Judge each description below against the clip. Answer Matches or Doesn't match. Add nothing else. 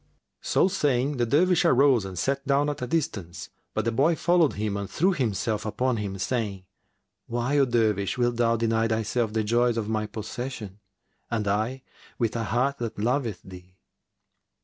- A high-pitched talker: Doesn't match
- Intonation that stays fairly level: Doesn't match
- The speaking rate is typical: Matches